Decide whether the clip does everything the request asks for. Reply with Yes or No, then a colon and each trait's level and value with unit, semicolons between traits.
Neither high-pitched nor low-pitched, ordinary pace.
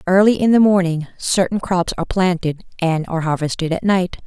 Yes: medium, 180 Hz; average, 185 wpm